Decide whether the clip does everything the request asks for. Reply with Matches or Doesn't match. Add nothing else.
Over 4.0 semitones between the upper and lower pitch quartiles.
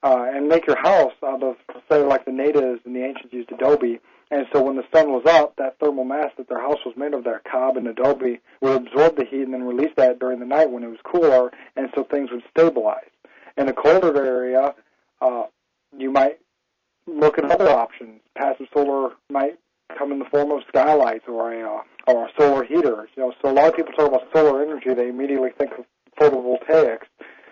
Doesn't match